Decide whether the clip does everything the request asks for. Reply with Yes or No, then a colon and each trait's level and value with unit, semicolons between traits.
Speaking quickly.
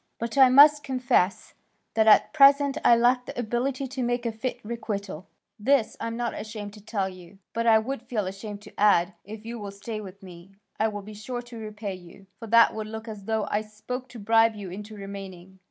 Yes: fast, 220 wpm